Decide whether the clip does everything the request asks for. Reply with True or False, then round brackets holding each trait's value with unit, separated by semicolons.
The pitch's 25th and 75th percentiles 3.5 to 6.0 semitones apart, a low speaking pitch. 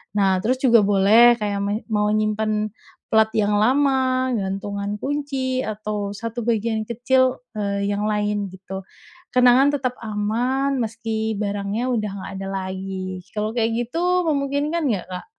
False (3.9 semitones; 215 Hz)